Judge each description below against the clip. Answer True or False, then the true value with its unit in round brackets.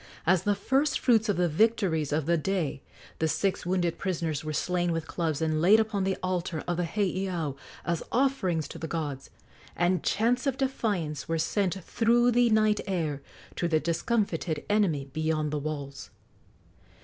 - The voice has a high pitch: False (175 Hz)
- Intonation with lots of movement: False (4.7 semitones)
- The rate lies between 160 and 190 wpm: True (170 wpm)